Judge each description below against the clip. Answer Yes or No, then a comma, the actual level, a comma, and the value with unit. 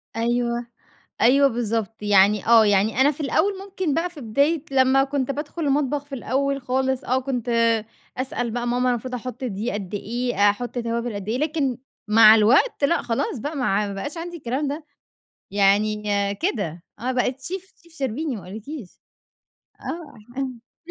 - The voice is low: No, very high, 250 Hz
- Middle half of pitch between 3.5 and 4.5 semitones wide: Yes, average, 4.1 semitones